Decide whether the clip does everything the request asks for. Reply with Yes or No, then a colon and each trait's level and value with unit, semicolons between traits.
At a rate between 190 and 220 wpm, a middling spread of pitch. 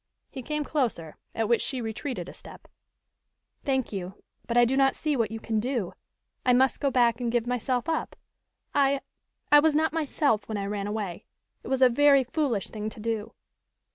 Yes: average, 195 wpm; average, 4.0 semitones